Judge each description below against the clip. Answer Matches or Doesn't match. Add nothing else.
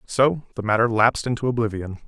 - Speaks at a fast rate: Doesn't match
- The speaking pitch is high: Doesn't match